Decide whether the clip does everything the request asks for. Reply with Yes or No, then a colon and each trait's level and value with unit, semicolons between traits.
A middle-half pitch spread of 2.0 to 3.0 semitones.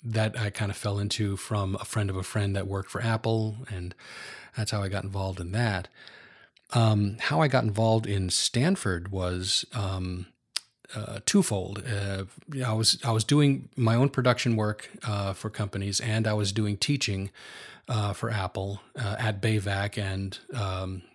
Yes: narrow, 2.5 semitones